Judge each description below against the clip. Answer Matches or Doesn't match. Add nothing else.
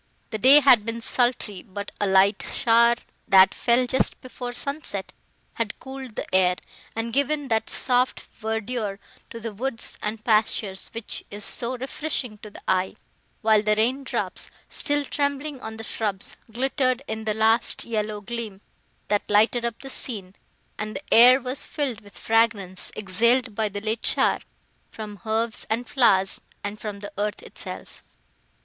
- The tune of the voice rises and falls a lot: Doesn't match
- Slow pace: Doesn't match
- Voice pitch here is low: Doesn't match